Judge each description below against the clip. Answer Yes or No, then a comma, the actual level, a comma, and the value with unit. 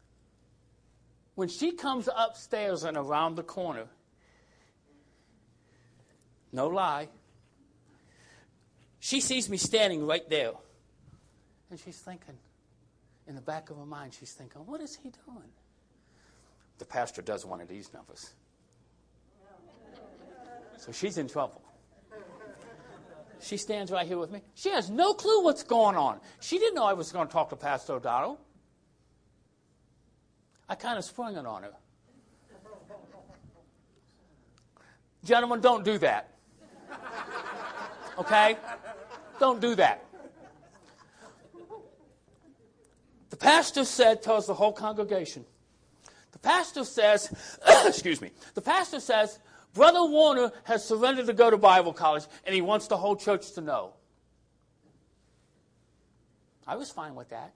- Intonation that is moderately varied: No, wide, 6.5 semitones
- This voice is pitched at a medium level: No, high, 210 Hz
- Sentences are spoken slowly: Yes, slow, 125 wpm